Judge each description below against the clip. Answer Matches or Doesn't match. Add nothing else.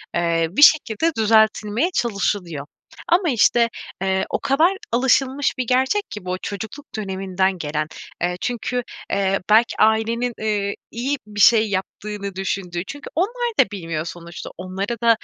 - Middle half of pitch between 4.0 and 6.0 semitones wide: Matches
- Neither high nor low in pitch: Doesn't match